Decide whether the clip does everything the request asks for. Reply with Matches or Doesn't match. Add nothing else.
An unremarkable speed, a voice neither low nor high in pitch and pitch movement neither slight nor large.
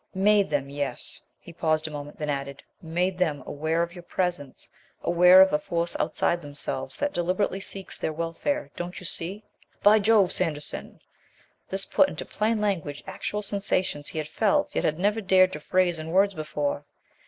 Matches